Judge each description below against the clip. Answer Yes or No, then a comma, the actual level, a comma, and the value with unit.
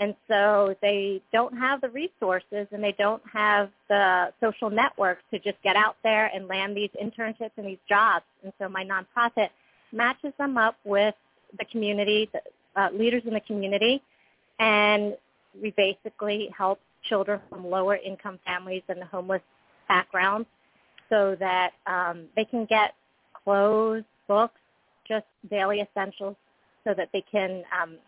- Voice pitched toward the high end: Yes, high, 205 Hz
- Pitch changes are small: Yes, narrow, 2.2 semitones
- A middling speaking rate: Yes, average, 150 wpm